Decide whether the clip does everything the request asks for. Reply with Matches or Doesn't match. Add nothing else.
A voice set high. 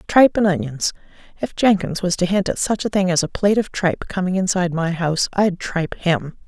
Doesn't match